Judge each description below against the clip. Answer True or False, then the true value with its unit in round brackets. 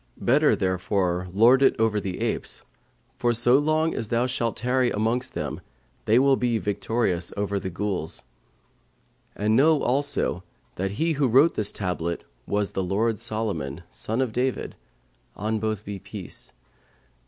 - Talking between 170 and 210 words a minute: False (150 wpm)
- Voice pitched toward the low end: True (110 Hz)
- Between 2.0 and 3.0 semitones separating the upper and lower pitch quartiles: False (4.2 semitones)